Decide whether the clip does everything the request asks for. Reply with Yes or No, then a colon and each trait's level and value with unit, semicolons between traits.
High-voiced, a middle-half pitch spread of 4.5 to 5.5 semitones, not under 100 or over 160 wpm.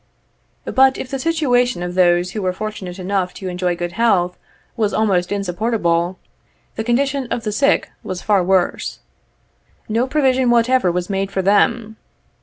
Yes: high, 205 Hz; average, 5.1 semitones; average, 155 wpm